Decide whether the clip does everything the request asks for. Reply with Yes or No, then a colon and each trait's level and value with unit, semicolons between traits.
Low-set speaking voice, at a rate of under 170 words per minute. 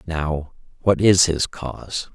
Yes: very low, 80 Hz; average, 140 wpm